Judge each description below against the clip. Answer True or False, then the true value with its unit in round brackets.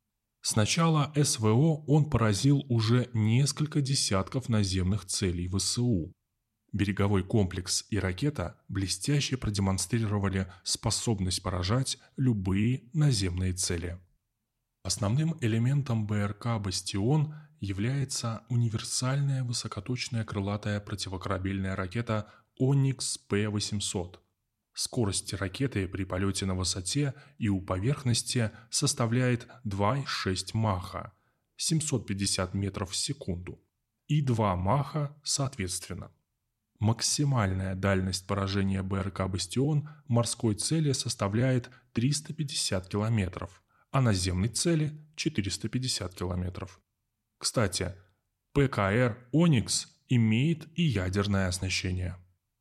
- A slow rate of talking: True (85 wpm)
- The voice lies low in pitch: True (110 Hz)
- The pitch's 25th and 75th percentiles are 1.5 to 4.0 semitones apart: False (4.9 semitones)